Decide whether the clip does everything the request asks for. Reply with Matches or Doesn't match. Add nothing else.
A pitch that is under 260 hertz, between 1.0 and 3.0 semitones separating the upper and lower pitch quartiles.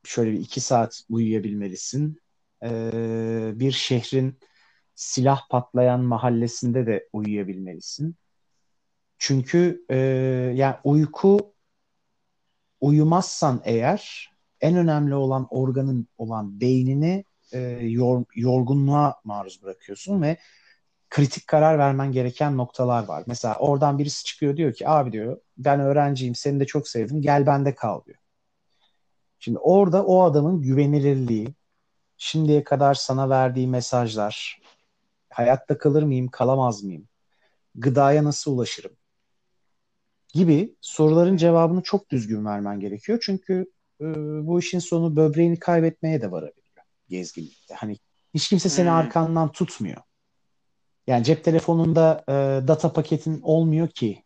Doesn't match